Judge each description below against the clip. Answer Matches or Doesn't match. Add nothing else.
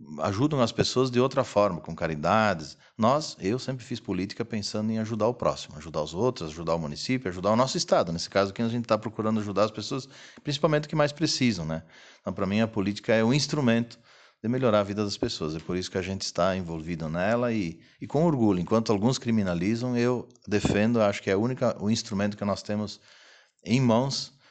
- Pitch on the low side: Matches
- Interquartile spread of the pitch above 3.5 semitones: Matches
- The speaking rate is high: Matches